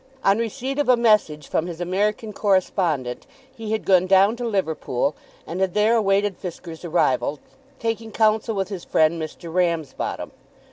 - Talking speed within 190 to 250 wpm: No, average, 155 wpm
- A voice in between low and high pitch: No, high, 195 Hz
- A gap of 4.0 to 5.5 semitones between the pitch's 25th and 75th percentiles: Yes, average, 4.5 semitones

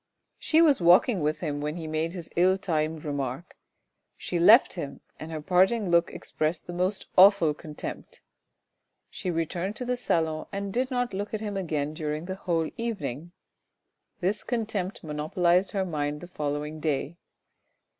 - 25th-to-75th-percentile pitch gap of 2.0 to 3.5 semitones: No, average, 4.2 semitones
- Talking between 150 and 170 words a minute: Yes, average, 160 wpm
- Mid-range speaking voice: Yes, medium, 175 Hz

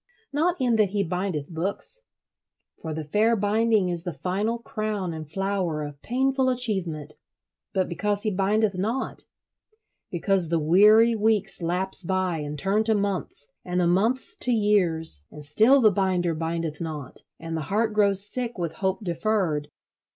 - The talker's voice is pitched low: No, high, 190 Hz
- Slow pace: No, average, 150 wpm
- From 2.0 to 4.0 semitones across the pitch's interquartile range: No, average, 4.5 semitones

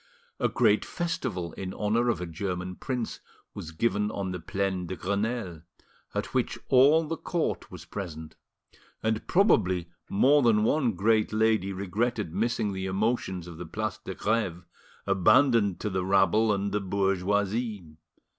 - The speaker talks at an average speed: Yes, average, 150 wpm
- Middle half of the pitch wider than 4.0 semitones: No, average, 3.7 semitones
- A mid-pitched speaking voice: No, low, 100 Hz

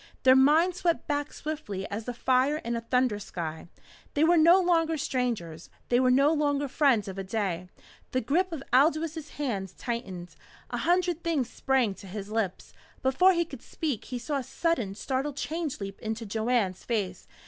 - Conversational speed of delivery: Yes, average, 180 wpm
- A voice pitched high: Yes, very high, 255 Hz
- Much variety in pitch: Yes, wide, 6.5 semitones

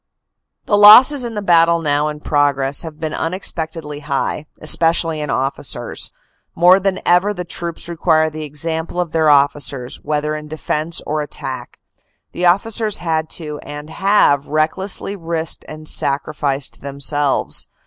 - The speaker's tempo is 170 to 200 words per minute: No, average, 150 wpm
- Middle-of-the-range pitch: Yes, medium, 155 Hz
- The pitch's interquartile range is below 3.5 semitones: Yes, average, 2.9 semitones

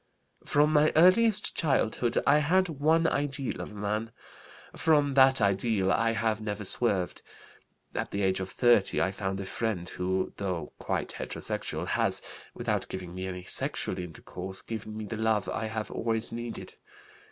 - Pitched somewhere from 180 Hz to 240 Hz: No, low, 110 Hz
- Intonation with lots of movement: Yes, wide, 6.3 semitones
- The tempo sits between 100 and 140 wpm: No, average, 160 wpm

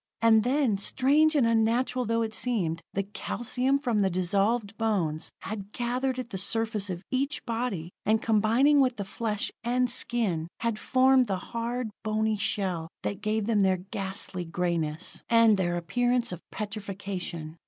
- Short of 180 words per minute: Yes, average, 155 wpm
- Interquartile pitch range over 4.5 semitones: No, average, 4.1 semitones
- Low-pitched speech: No, high, 220 Hz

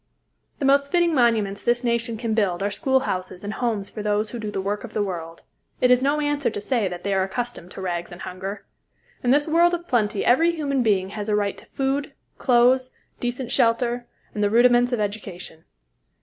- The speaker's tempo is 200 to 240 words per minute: Yes, fast, 205 wpm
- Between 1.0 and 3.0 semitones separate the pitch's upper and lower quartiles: No, average, 4.2 semitones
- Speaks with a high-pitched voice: Yes, high, 230 Hz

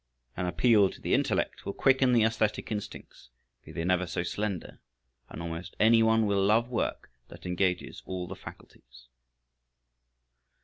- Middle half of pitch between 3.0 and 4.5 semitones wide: Yes, average, 4.0 semitones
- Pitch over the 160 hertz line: No, low, 100 Hz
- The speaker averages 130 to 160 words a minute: Yes, average, 150 wpm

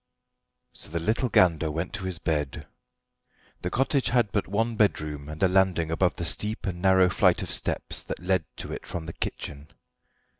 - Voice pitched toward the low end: Yes, very low, 90 Hz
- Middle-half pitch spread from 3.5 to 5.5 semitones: Yes, average, 3.9 semitones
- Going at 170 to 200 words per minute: Yes, average, 185 wpm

